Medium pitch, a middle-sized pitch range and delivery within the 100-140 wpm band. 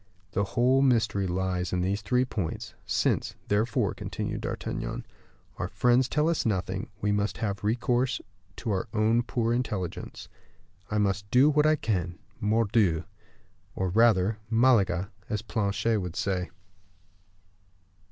No: low, 105 Hz; average, 3.7 semitones; slow, 135 wpm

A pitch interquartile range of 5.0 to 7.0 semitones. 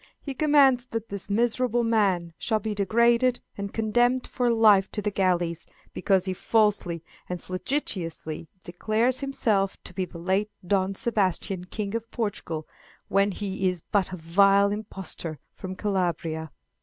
No: average, 3.8 semitones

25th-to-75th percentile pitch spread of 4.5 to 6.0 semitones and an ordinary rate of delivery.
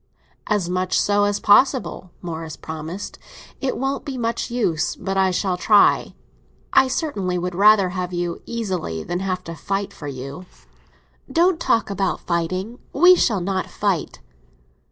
No: average, 3.9 semitones; average, 150 wpm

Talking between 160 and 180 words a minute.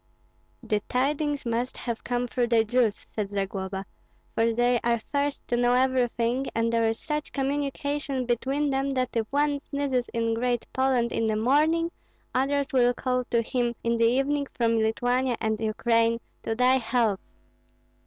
Yes: average, 165 wpm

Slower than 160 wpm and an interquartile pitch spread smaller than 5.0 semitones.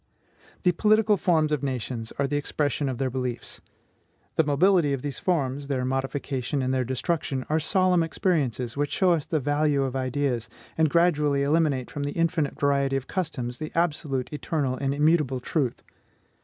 No: average, 170 wpm; average, 3.4 semitones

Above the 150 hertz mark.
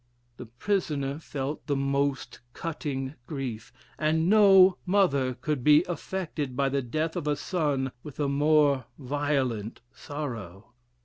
No: medium, 145 Hz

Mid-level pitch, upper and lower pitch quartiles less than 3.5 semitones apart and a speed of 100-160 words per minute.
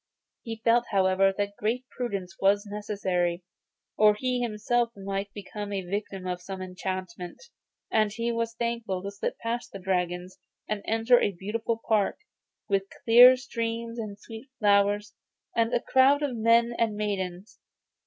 No: high, 210 Hz; average, 3.0 semitones; average, 150 wpm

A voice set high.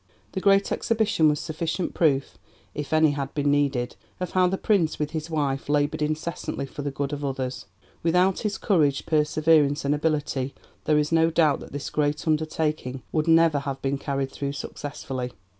No: medium, 150 Hz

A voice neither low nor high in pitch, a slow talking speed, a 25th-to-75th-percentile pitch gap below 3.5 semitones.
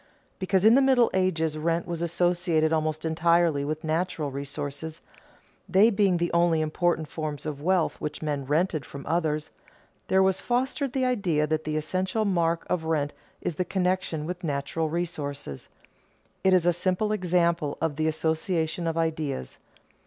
No: medium, 165 Hz; average, 160 wpm; average, 2.9 semitones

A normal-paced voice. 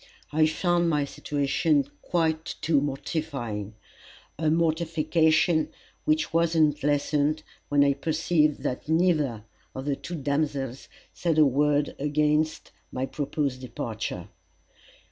No: slow, 115 wpm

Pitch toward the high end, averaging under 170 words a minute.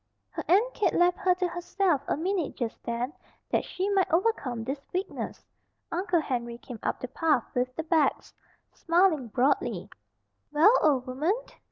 Yes: very high, 320 Hz; average, 160 wpm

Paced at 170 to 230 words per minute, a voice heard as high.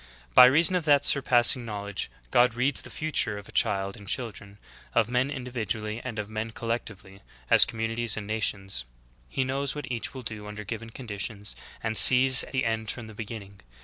No: average, 185 wpm; low, 115 Hz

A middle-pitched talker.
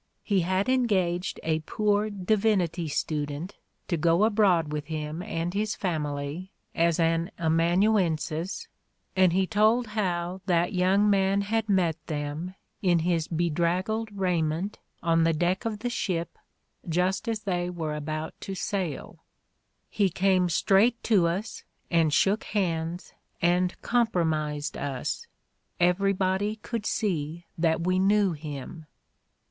Yes: medium, 180 Hz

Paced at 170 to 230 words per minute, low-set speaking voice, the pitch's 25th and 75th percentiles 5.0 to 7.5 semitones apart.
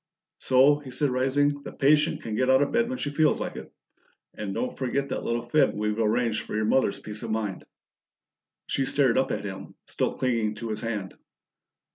No: average, 200 wpm; low, 125 Hz; average, 4.4 semitones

